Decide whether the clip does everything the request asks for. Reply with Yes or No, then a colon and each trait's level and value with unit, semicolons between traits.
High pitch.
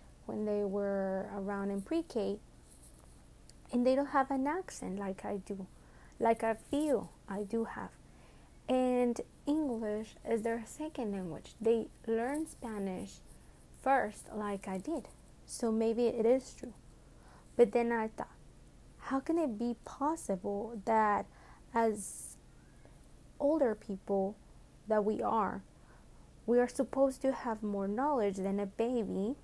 Yes: high, 220 Hz